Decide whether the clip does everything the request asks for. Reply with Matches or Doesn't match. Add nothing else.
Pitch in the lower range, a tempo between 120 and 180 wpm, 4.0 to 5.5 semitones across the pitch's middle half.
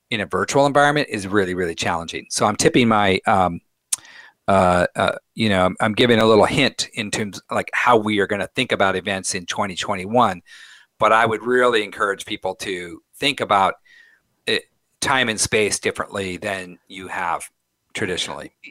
Matches